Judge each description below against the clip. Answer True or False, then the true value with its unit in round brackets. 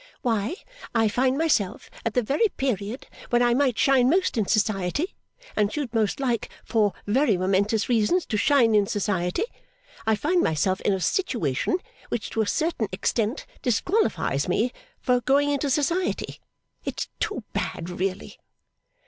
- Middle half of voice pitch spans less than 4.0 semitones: False (5.3 semitones)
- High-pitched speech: True (230 Hz)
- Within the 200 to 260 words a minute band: False (150 wpm)